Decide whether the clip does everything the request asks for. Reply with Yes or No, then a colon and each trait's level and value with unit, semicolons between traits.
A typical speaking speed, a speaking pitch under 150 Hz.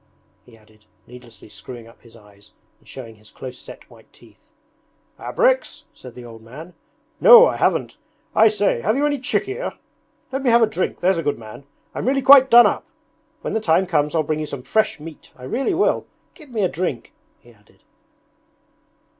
No: average, 190 wpm; medium, 160 Hz